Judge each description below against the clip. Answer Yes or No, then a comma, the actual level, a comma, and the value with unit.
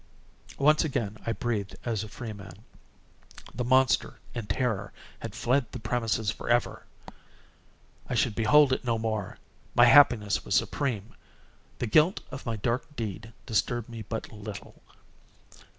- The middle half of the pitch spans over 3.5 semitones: No, average, 2.8 semitones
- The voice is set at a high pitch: No, low, 115 Hz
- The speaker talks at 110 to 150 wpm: Yes, slow, 135 wpm